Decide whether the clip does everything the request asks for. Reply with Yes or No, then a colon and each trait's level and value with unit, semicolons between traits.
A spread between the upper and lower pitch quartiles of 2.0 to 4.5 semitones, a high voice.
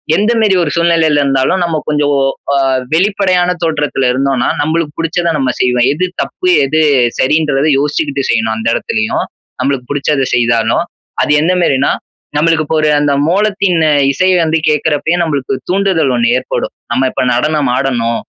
No: average, 4.0 semitones; medium, 150 Hz